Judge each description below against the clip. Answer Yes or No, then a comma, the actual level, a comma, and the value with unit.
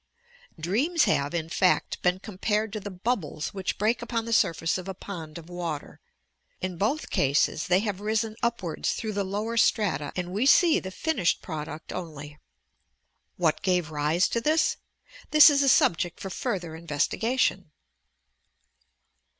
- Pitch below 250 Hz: Yes, high, 190 Hz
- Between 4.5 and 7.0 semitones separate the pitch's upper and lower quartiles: Yes, average, 5.2 semitones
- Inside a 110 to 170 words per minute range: Yes, average, 150 wpm